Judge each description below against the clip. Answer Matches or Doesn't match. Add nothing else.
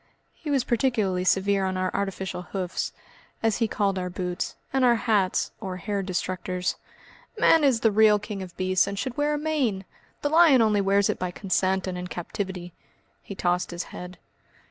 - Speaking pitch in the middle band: Doesn't match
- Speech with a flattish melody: Doesn't match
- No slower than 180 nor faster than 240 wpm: Matches